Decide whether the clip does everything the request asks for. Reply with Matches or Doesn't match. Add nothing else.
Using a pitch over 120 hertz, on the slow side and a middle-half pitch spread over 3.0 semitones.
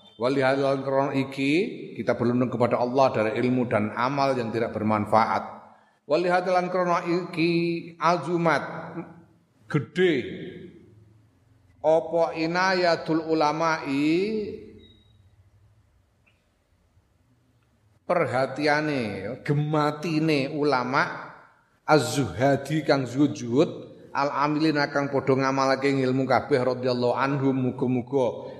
Matches